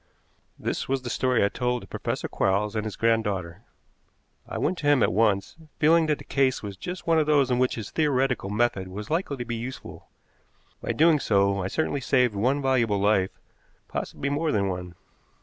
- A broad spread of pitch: Yes, wide, 5.7 semitones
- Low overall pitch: Yes, low, 120 Hz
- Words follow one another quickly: No, average, 195 wpm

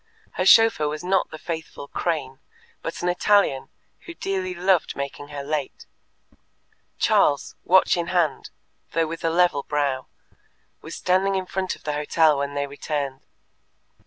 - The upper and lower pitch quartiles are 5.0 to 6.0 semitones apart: No, average, 4.2 semitones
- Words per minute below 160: Yes, average, 150 wpm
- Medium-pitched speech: Yes, medium, 160 Hz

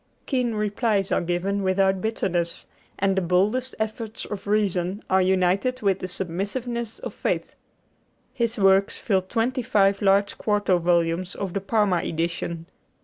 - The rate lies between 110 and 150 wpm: Yes, average, 145 wpm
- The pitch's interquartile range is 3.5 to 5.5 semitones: No, average, 2.9 semitones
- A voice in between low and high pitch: No, high, 195 Hz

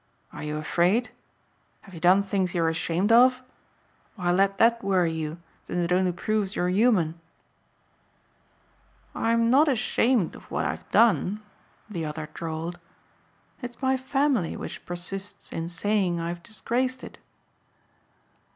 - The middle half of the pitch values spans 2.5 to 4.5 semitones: No, average, 5.2 semitones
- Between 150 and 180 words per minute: No, slow, 135 wpm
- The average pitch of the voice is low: No, high, 190 Hz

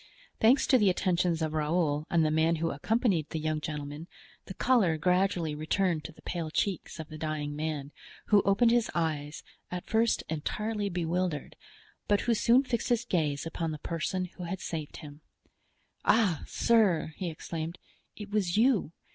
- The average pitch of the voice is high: No, medium, 170 Hz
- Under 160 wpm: No, average, 170 wpm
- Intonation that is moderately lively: Yes, average, 4.5 semitones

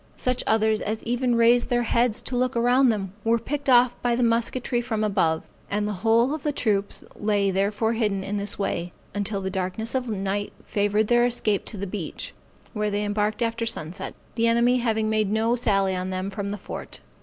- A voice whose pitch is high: Yes, high, 220 Hz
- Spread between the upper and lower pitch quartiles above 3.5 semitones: No, average, 2.9 semitones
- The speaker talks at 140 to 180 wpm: No, fast, 205 wpm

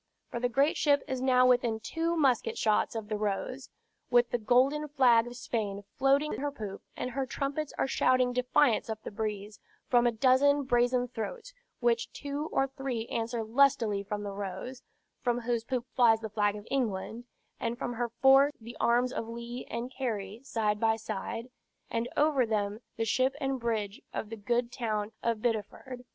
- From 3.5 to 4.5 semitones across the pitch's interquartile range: No, average, 3.0 semitones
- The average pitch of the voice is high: Yes, high, 240 Hz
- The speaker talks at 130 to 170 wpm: No, average, 185 wpm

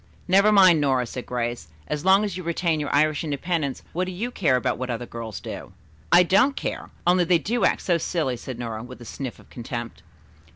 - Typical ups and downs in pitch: No, wide, 6.6 semitones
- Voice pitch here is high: No, medium, 150 Hz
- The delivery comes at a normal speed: No, fast, 215 wpm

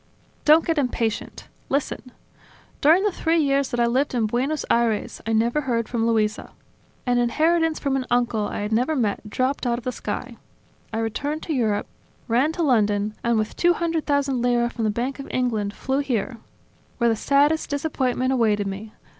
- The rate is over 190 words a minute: No, average, 185 wpm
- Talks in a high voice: Yes, high, 245 Hz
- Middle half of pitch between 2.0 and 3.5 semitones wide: No, average, 4.0 semitones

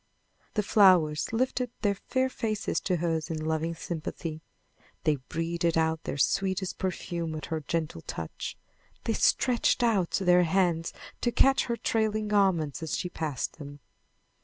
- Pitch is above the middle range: No, medium, 170 Hz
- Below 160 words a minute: Yes, average, 145 wpm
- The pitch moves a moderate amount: Yes, average, 4.6 semitones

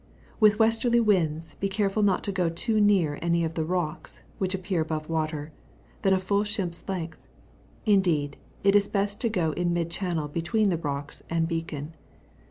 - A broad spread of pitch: No, average, 3.8 semitones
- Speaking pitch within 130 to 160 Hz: No, medium, 180 Hz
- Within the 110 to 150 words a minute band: No, average, 180 wpm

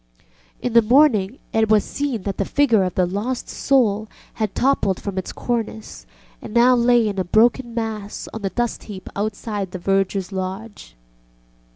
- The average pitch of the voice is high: Yes, high, 215 Hz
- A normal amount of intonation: Yes, average, 3.5 semitones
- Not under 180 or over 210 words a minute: No, average, 170 wpm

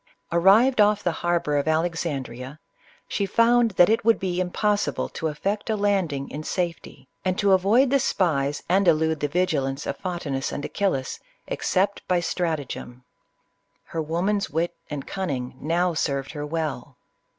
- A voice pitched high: No, medium, 170 Hz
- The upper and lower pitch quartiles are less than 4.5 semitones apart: No, average, 5.1 semitones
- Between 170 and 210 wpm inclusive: No, average, 155 wpm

